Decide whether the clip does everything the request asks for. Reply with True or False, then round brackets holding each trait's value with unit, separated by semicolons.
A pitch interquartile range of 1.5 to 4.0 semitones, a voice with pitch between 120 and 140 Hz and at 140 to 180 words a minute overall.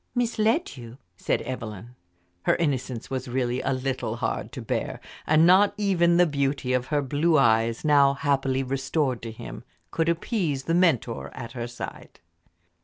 False (4.8 semitones; 135 Hz; 160 wpm)